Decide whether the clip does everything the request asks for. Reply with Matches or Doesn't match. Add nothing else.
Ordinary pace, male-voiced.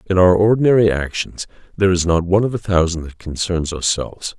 Matches